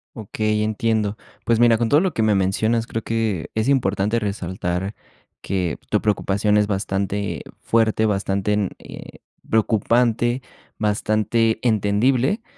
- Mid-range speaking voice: No, low, 110 Hz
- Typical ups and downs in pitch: No, narrow, 2.3 semitones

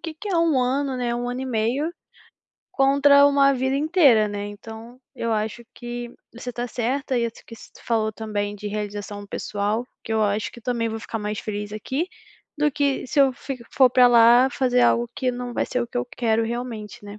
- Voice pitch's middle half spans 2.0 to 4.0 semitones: Yes, average, 3.2 semitones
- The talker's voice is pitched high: Yes, high, 240 Hz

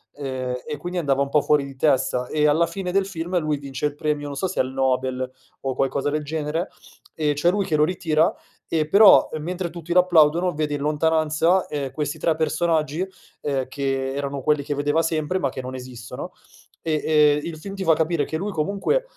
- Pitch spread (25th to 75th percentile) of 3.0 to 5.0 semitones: Yes, average, 3.4 semitones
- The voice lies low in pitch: No, medium, 150 Hz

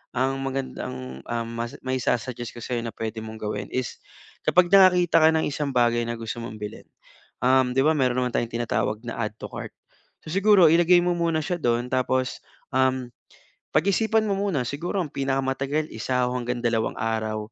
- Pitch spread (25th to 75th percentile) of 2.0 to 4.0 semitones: No, average, 5.2 semitones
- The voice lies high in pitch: No, low, 130 Hz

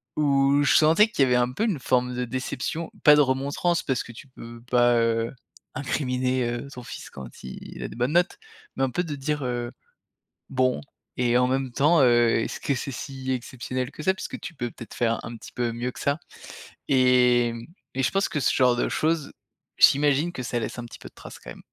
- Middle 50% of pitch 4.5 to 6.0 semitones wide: No, average, 2.9 semitones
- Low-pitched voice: Yes, low, 130 Hz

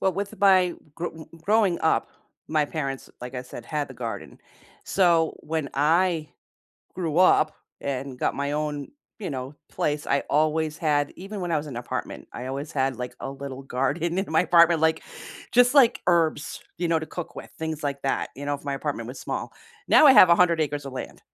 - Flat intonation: No, average, 3.6 semitones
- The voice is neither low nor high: Yes, medium, 155 Hz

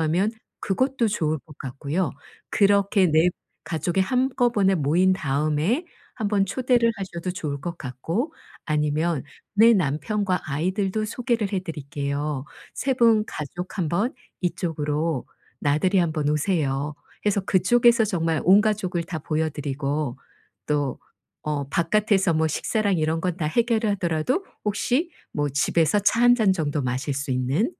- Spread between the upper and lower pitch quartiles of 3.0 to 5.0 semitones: No, wide, 5.6 semitones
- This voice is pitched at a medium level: Yes, medium, 175 Hz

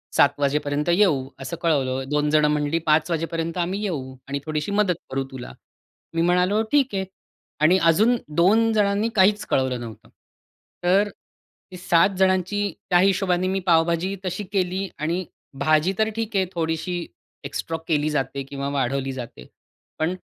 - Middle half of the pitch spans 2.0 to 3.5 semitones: No, average, 4.5 semitones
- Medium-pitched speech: Yes, medium, 170 Hz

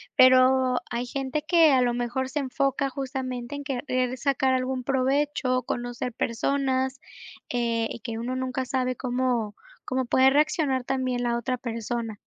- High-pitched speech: Yes, very high, 255 Hz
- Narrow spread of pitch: Yes, narrow, 1.7 semitones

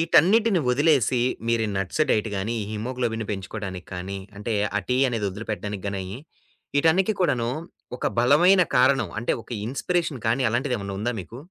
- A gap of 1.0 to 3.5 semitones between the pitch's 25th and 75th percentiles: No, wide, 5.5 semitones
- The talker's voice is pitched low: Yes, low, 120 Hz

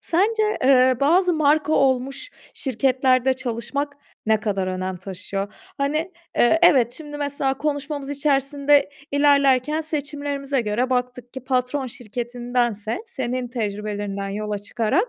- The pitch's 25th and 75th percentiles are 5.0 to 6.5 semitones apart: No, average, 3.5 semitones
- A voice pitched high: Yes, very high, 260 Hz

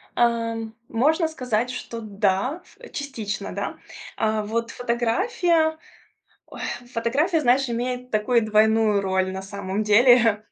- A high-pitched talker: Yes, high, 230 Hz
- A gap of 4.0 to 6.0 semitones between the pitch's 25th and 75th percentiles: No, average, 3.1 semitones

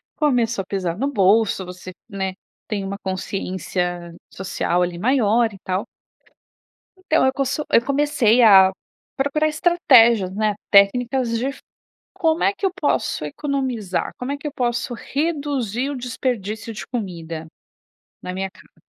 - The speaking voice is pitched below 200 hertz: No, high, 230 Hz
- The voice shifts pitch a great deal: Yes, wide, 6.2 semitones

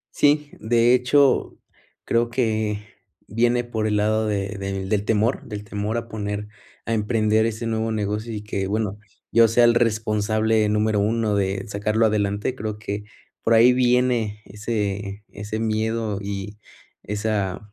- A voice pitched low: Yes, low, 110 Hz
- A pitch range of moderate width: No, narrow, 1.8 semitones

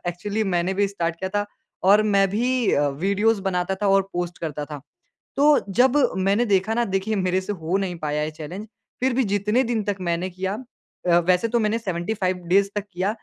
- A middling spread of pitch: Yes, average, 3.1 semitones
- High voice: Yes, high, 195 Hz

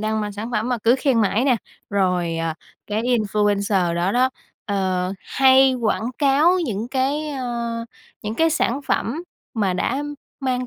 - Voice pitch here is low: No, high, 230 Hz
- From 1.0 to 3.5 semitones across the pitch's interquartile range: No, average, 4.5 semitones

